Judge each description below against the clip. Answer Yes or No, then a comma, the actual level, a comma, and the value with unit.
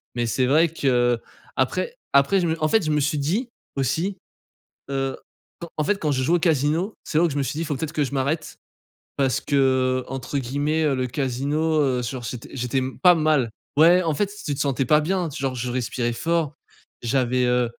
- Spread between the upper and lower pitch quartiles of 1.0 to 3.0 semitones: No, average, 3.8 semitones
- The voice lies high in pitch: No, medium, 140 Hz